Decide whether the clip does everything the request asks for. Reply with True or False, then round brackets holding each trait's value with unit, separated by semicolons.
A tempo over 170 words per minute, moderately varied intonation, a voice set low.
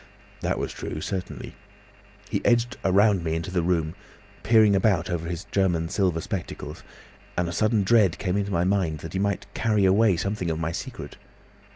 True (180 wpm; 3.3 semitones; 95 Hz)